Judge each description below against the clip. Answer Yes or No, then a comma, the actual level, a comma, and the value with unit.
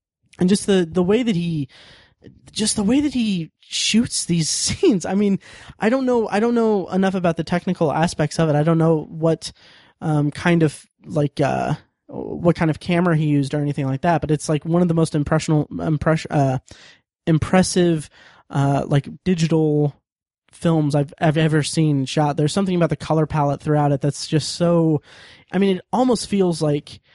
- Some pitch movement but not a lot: Yes, average, 3.6 semitones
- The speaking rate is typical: Yes, average, 190 wpm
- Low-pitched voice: No, medium, 160 Hz